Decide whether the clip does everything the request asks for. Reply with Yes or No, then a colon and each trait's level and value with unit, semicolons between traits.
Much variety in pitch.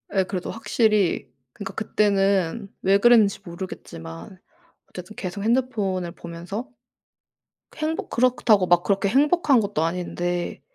No: average, 4.1 semitones